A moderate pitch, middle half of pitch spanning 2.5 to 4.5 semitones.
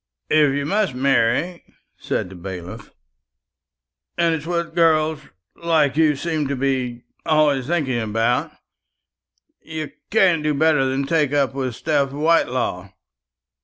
Yes: medium, 145 Hz; average, 3.6 semitones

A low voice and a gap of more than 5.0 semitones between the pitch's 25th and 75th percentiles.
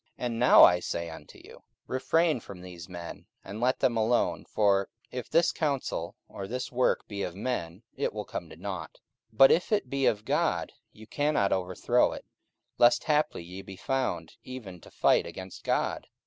Yes: low, 110 Hz; wide, 5.6 semitones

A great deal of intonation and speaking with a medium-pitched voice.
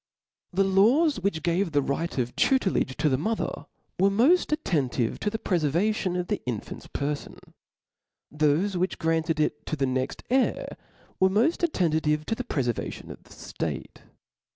Yes: wide, 5.7 semitones; medium, 175 Hz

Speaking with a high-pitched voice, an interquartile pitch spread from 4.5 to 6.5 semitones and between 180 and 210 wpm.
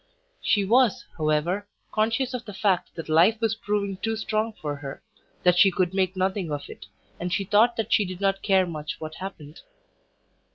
No: high, 195 Hz; average, 3.7 semitones; average, 190 wpm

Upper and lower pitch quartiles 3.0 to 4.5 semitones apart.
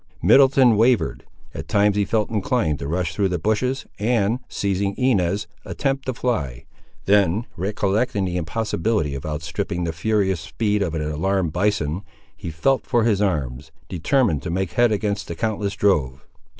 No: average, 5.1 semitones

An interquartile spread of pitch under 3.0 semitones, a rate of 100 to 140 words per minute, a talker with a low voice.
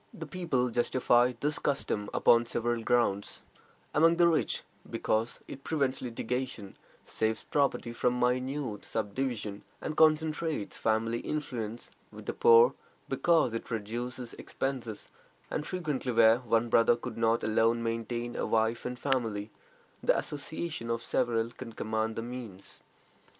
No: average, 3.3 semitones; slow, 135 wpm; low, 120 Hz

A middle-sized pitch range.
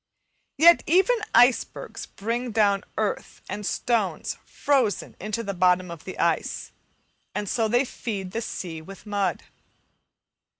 Yes: average, 3.9 semitones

